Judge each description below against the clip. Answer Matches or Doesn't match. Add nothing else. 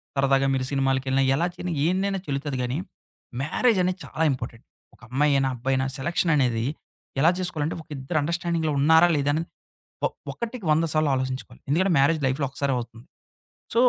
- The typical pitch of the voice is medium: Matches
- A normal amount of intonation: Matches